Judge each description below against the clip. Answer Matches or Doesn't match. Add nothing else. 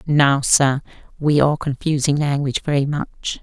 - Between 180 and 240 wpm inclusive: Doesn't match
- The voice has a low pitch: Doesn't match